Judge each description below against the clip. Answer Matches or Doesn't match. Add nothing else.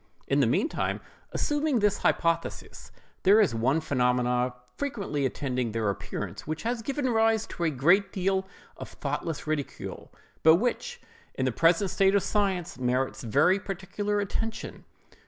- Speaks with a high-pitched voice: Doesn't match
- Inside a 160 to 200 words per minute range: Doesn't match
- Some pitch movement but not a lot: Doesn't match